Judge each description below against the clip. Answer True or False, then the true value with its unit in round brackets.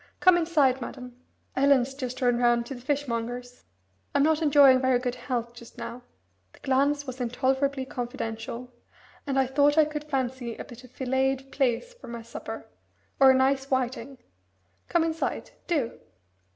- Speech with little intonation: True (2.3 semitones)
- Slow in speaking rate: False (160 wpm)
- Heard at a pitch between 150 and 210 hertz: False (260 Hz)